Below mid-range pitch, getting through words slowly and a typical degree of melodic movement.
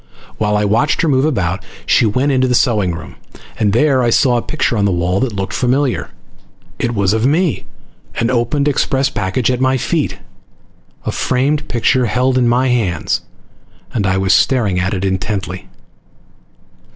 No: low, 120 Hz; average, 175 wpm; average, 4.7 semitones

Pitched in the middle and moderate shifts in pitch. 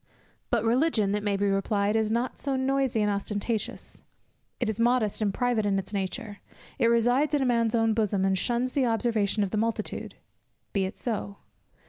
No: high, 220 Hz; average, 3.1 semitones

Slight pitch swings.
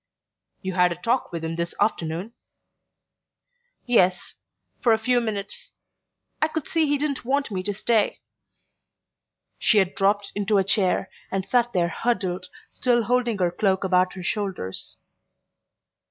No: average, 4.5 semitones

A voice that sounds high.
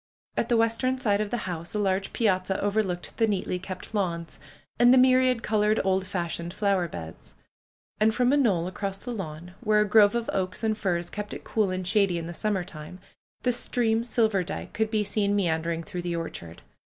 Yes: high, 200 Hz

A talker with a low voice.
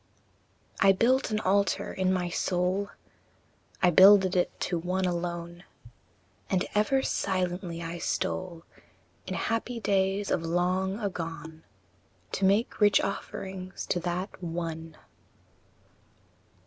No: medium, 185 Hz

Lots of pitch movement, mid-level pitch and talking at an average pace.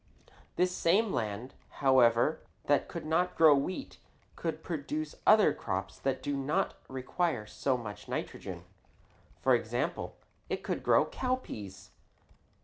No: wide, 5.8 semitones; medium, 145 Hz; slow, 125 wpm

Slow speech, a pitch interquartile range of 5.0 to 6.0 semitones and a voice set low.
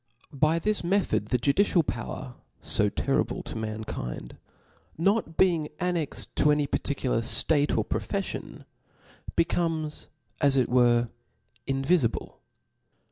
No: slow, 115 wpm; wide, 5.4 semitones; medium, 145 Hz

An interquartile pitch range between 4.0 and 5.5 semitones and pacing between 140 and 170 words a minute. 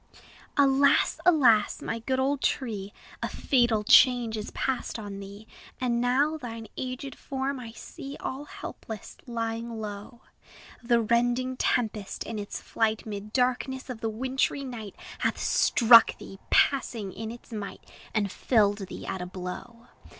No: average, 3.4 semitones; average, 145 wpm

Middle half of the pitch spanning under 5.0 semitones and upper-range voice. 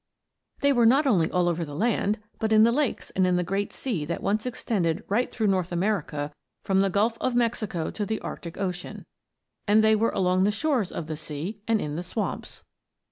Yes: average, 4.2 semitones; high, 200 Hz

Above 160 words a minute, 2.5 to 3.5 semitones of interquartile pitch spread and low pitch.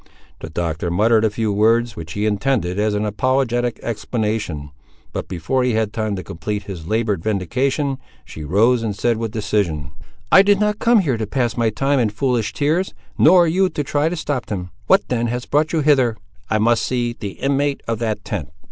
No: average, 200 wpm; average, 4.7 semitones; low, 115 Hz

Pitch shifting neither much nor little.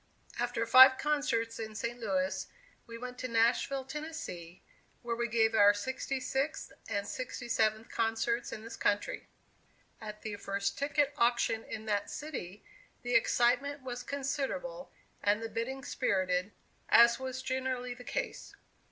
Yes: average, 3.1 semitones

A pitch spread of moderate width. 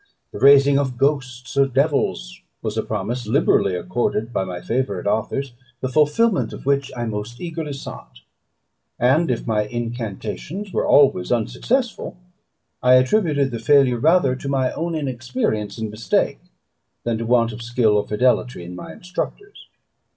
Yes: average, 4.2 semitones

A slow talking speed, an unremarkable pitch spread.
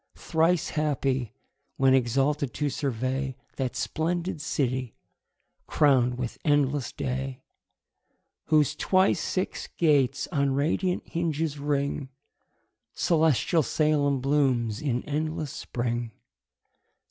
Yes: slow, 95 wpm; average, 3.0 semitones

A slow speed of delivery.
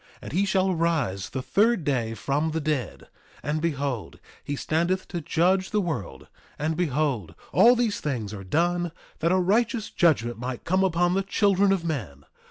No: average, 180 wpm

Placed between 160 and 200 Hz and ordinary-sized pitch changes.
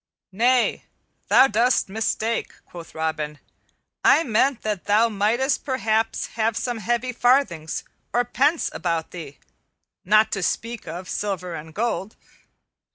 No: high, 220 Hz; average, 4.9 semitones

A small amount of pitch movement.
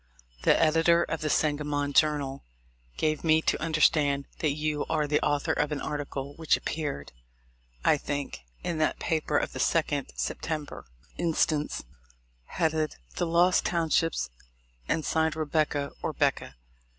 Yes: narrow, 1.7 semitones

